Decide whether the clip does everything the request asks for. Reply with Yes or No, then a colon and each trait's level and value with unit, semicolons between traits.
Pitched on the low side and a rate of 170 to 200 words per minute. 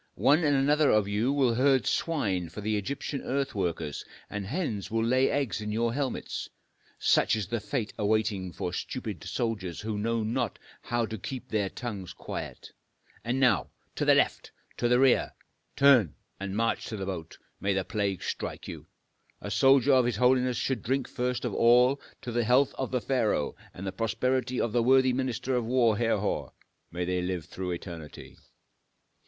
Yes: low, 115 Hz; average, 180 wpm